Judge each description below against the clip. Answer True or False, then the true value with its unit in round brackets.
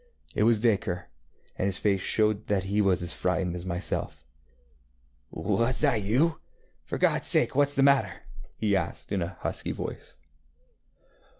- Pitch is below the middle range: True (100 Hz)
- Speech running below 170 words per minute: True (155 wpm)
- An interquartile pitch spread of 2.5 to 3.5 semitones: False (4.0 semitones)